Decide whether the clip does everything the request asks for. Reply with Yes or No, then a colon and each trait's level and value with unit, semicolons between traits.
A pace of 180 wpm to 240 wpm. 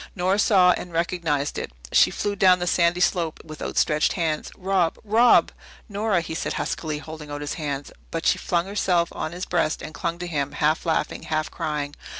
Yes: average, 190 wpm